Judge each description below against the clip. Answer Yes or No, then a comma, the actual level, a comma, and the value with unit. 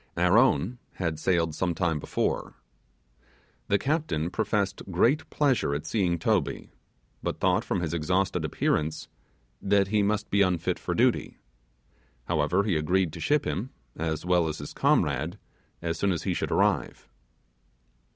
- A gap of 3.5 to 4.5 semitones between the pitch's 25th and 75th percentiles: Yes, average, 4.1 semitones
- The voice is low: Yes, very low, 90 Hz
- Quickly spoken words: No, average, 150 wpm